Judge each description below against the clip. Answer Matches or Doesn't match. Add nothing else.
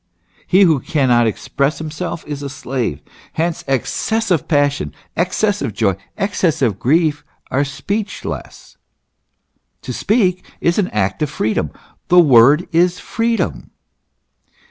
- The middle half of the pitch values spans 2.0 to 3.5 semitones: Doesn't match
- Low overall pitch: Doesn't match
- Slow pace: Matches